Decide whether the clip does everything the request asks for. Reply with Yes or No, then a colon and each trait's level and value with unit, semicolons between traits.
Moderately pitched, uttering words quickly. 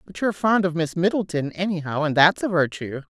Yes: medium, 175 Hz; fast, 210 wpm